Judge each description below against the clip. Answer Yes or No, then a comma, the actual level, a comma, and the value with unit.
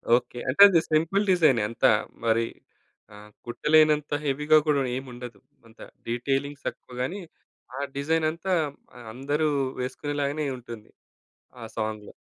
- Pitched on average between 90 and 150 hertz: Yes, medium, 140 Hz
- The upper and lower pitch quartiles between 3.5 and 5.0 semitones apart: Yes, average, 4.2 semitones